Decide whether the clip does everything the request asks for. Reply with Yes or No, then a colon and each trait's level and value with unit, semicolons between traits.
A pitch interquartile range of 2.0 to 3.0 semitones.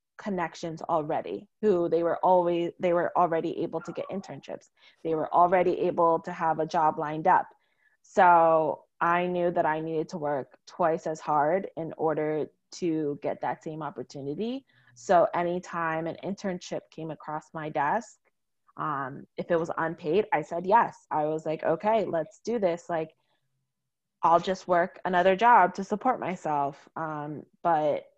Yes: narrow, 2.4 semitones